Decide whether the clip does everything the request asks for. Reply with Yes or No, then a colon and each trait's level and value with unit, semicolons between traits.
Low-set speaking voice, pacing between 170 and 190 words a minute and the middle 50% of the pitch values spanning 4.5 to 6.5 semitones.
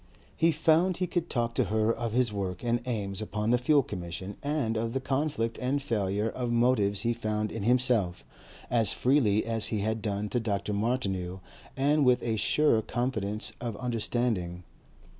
No: low, 115 Hz; average, 175 wpm; average, 3.5 semitones